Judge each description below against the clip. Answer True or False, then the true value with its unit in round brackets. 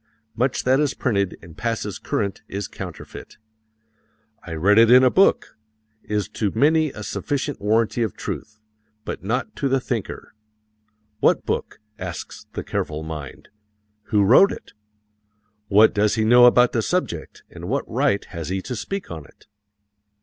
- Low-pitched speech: True (110 Hz)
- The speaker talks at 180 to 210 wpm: False (155 wpm)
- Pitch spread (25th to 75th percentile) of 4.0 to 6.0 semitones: True (4.6 semitones)